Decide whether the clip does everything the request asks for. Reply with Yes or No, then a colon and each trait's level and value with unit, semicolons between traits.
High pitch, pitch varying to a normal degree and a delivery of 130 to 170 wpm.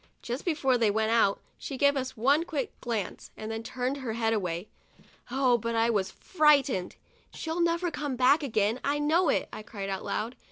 No: very high, 250 Hz; average, 4.5 semitones; average, 195 wpm